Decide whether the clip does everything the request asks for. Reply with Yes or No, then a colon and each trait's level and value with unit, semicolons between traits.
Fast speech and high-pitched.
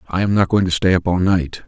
No: fast, 325 wpm; very low, 90 Hz